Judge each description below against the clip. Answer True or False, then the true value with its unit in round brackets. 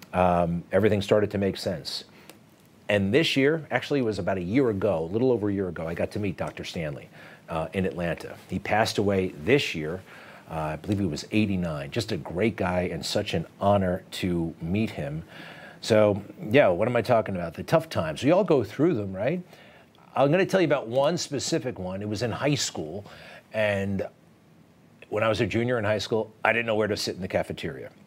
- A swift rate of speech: True (215 wpm)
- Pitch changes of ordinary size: True (4.3 semitones)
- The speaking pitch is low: True (105 Hz)